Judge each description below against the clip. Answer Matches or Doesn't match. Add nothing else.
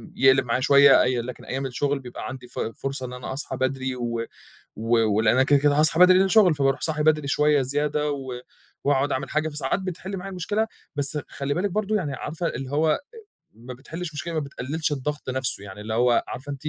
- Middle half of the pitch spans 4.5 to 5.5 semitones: Doesn't match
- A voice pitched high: Doesn't match